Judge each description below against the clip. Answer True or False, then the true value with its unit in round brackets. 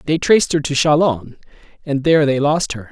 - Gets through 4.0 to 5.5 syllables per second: False (5.7 syllables/s)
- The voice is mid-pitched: True (145 Hz)